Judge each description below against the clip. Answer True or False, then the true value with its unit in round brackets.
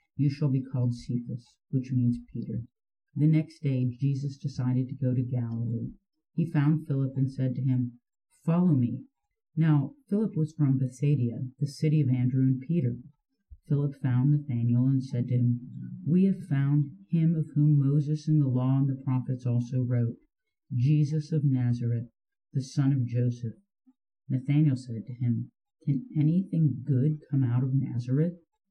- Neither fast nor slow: True (160 wpm)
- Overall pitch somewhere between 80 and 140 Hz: True (135 Hz)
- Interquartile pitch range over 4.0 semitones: False (3.4 semitones)